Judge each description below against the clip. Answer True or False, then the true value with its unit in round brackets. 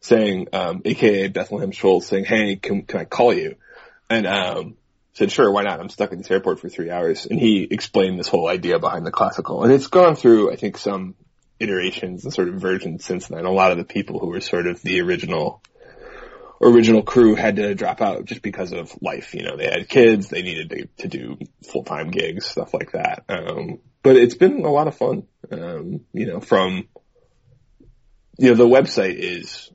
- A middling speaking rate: False (210 wpm)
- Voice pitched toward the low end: True (120 Hz)